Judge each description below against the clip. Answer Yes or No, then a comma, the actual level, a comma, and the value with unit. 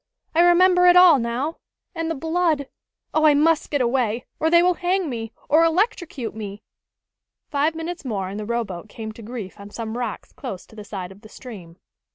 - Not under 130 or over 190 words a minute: No, average, 200 wpm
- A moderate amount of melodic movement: No, wide, 7.1 semitones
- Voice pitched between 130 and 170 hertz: No, very high, 265 Hz